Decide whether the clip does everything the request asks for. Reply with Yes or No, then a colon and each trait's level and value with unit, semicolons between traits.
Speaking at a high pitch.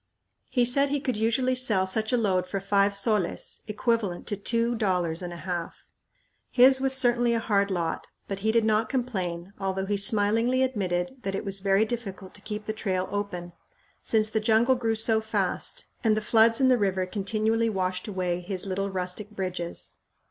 Yes: high, 210 Hz